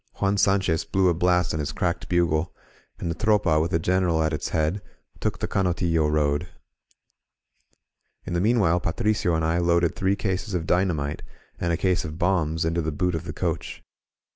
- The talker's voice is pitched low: Yes, very low, 85 Hz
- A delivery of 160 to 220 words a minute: Yes, average, 185 wpm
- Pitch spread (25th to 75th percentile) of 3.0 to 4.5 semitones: No, narrow, 2.5 semitones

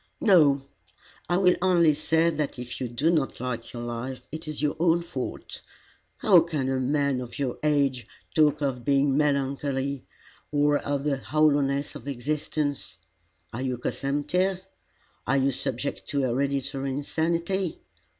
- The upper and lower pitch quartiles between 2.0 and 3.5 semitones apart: Yes, narrow, 2.6 semitones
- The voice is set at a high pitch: No, medium, 140 Hz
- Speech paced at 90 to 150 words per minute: Yes, average, 145 wpm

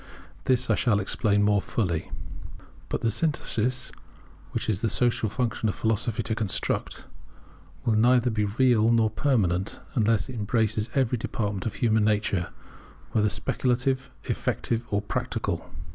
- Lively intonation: No, average, 2.8 semitones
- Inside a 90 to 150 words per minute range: Yes, average, 145 wpm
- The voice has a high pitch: No, low, 110 Hz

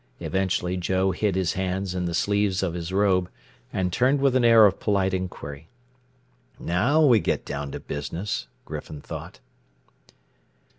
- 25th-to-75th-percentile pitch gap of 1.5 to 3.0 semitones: Yes, average, 2.7 semitones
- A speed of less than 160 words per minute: Yes, average, 150 wpm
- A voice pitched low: Yes, very low, 95 Hz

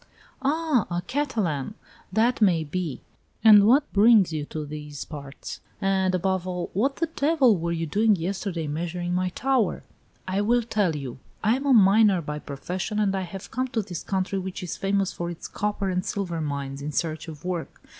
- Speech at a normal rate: Yes, average, 185 wpm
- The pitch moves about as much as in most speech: Yes, average, 4.7 semitones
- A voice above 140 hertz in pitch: Yes, medium, 185 Hz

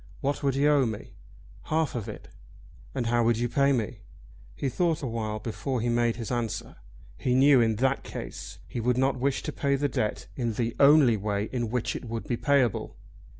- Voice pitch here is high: No, low, 120 Hz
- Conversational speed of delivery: No, fast, 210 wpm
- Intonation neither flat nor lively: Yes, average, 3.2 semitones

